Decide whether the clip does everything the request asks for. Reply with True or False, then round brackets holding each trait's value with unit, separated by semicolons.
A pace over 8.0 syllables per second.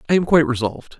True (8.9 syllables/s)